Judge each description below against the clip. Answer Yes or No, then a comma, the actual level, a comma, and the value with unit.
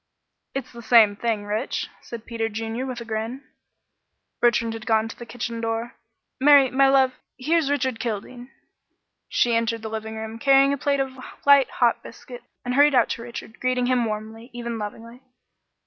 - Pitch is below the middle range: No, high, 235 Hz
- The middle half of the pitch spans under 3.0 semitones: Yes, narrow, 2.6 semitones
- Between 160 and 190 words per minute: Yes, average, 175 wpm